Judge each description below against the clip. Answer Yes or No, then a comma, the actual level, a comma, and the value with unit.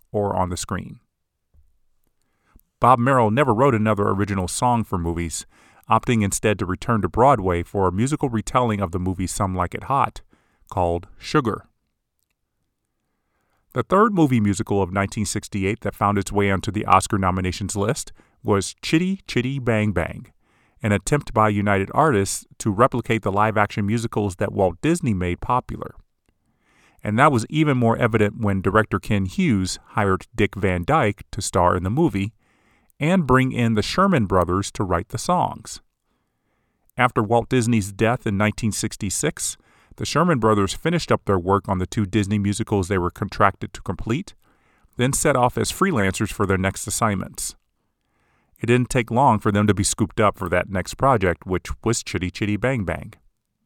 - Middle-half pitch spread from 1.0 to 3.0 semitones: No, average, 3.6 semitones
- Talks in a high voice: No, low, 105 Hz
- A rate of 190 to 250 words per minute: No, average, 165 wpm